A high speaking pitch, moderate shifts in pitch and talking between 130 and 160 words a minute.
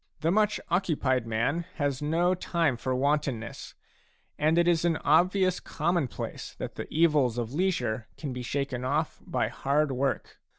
No: medium, 150 Hz; average, 4.8 semitones; average, 155 wpm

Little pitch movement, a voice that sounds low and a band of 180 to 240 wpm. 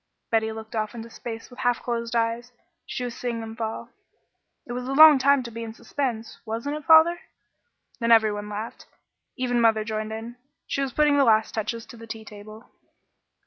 No: narrow, 2.2 semitones; high, 230 Hz; average, 200 wpm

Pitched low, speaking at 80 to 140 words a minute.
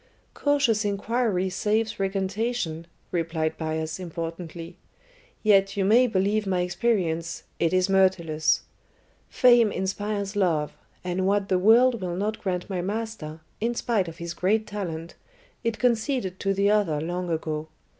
No: high, 190 Hz; slow, 135 wpm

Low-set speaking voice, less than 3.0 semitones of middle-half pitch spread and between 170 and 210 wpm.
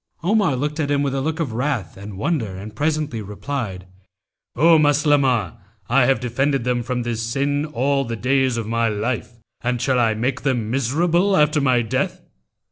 No: low, 130 Hz; average, 3.9 semitones; average, 180 wpm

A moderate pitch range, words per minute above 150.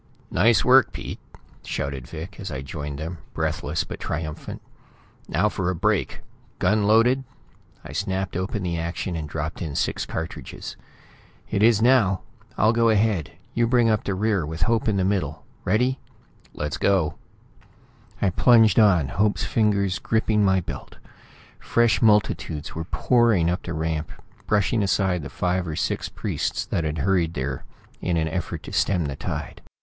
Yes: average, 4.9 semitones; average, 160 wpm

